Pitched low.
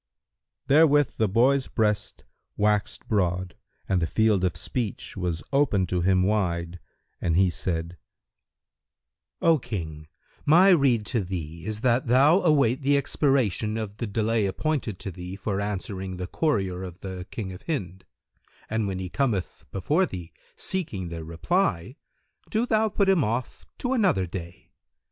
Yes: low, 105 Hz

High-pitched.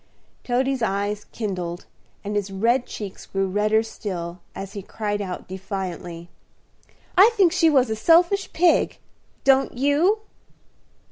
Yes: high, 210 Hz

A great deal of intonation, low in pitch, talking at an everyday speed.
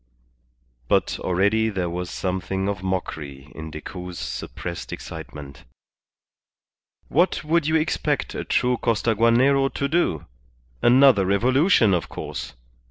No: wide, 6.9 semitones; low, 100 Hz; slow, 110 wpm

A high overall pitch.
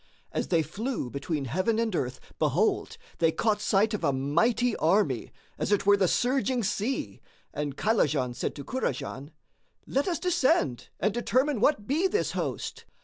Yes: high, 205 Hz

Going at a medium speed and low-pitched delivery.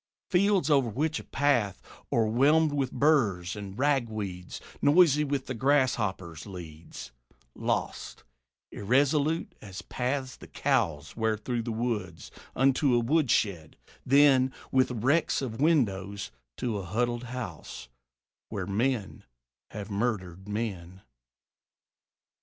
No: slow, 110 wpm; low, 120 Hz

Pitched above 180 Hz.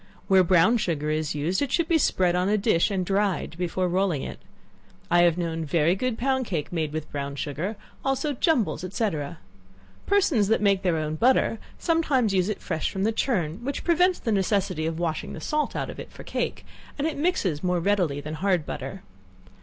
Yes: high, 190 Hz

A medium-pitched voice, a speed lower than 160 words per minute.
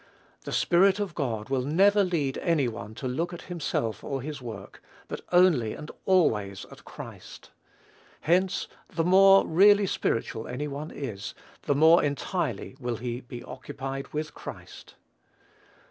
Yes: medium, 145 Hz; average, 145 wpm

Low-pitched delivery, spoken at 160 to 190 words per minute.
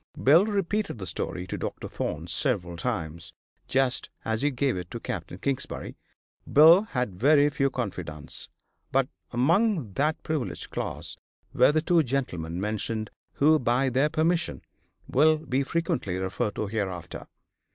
No: low, 130 Hz; average, 140 wpm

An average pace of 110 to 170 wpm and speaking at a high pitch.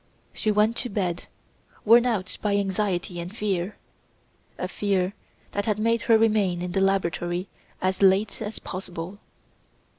Yes: average, 145 wpm; high, 195 Hz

